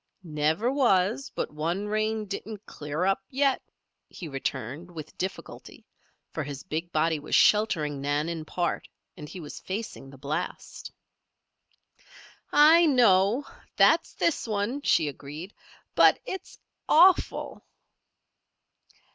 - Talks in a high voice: No, medium, 180 Hz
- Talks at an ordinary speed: No, slow, 120 wpm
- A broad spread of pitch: Yes, wide, 6.5 semitones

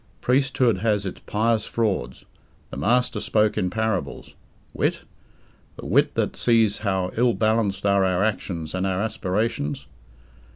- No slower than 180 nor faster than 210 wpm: No, slow, 135 wpm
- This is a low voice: Yes, low, 105 Hz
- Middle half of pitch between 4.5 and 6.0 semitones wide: No, average, 3.4 semitones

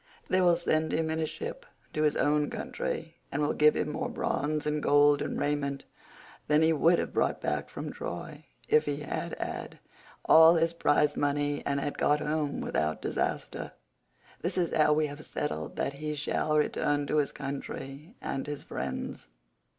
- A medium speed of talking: Yes, average, 180 wpm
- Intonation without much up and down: Yes, narrow, 1.7 semitones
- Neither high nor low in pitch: Yes, medium, 150 Hz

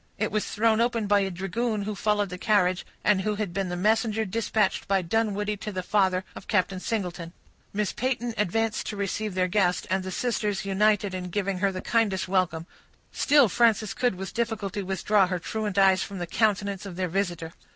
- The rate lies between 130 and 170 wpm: No, average, 195 wpm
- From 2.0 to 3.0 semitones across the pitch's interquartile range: Yes, narrow, 2.5 semitones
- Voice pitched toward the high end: Yes, high, 200 Hz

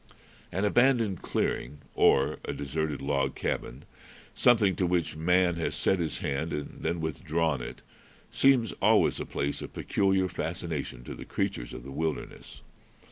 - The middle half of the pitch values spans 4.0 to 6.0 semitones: Yes, average, 4.7 semitones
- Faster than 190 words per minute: No, average, 150 wpm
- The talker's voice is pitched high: No, very low, 80 Hz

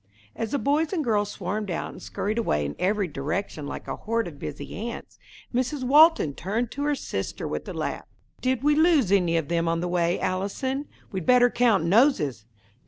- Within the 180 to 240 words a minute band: Yes, average, 195 wpm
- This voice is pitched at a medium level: No, high, 210 Hz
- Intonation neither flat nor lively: No, wide, 7.1 semitones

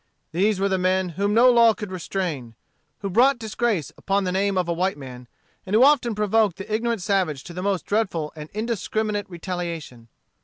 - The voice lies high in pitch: Yes, high, 195 Hz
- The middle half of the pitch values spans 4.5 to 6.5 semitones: No, average, 3.9 semitones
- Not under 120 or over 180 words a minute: No, average, 190 wpm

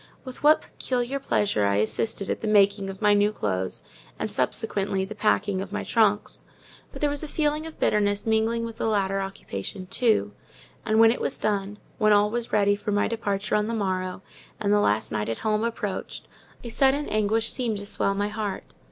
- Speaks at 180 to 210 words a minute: Yes, average, 195 wpm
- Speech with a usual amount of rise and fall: No, narrow, 2.3 semitones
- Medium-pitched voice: No, high, 210 Hz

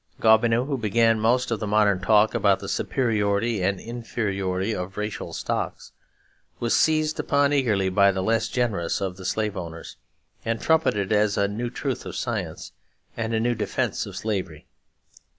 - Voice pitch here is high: No, low, 110 Hz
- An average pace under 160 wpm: No, average, 165 wpm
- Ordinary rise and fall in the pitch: Yes, average, 3.0 semitones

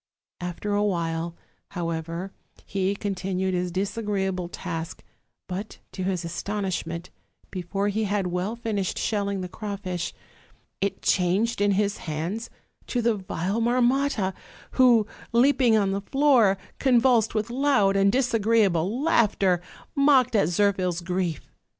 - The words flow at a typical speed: No, slow, 125 wpm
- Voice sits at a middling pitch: No, high, 200 Hz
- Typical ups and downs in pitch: Yes, average, 3.8 semitones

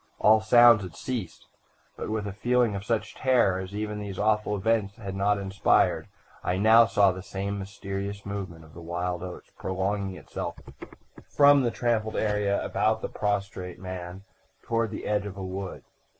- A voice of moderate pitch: No, low, 100 Hz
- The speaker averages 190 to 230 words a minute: No, average, 170 wpm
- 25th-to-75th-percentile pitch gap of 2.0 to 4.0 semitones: Yes, narrow, 2.4 semitones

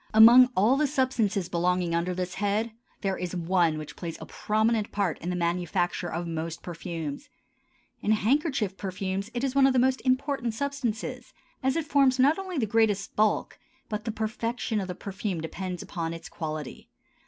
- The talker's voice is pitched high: Yes, high, 205 Hz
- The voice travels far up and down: Yes, wide, 5.9 semitones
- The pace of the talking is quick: No, average, 175 wpm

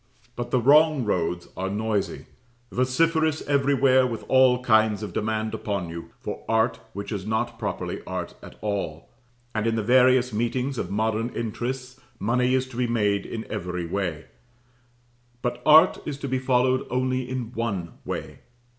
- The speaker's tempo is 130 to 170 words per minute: Yes, average, 160 wpm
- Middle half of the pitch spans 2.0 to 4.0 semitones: Yes, average, 3.6 semitones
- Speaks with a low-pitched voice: Yes, low, 120 Hz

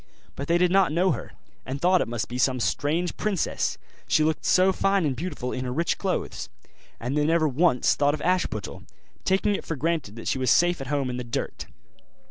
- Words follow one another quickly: Yes, fast, 215 wpm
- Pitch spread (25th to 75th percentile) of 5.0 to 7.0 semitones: Yes, wide, 5.6 semitones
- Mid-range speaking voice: Yes, medium, 155 Hz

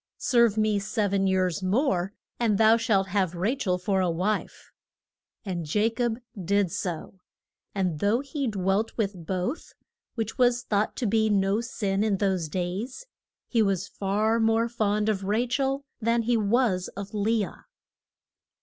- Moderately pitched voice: No, high, 205 Hz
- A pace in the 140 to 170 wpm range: Yes, average, 160 wpm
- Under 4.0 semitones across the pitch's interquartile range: Yes, average, 3.2 semitones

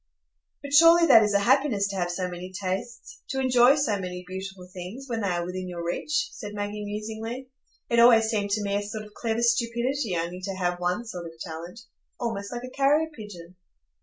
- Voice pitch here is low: No, high, 210 Hz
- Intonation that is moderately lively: Yes, average, 4.7 semitones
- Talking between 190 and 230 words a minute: Yes, average, 195 wpm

